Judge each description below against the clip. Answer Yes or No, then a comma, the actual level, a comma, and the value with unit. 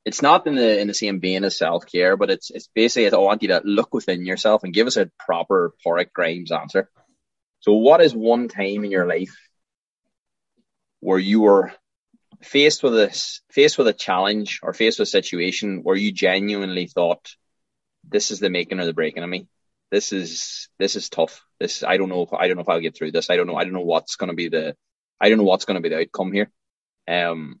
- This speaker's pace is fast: Yes, fast, 230 wpm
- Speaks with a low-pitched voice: Yes, low, 100 Hz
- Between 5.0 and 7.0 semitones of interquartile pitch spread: No, average, 2.8 semitones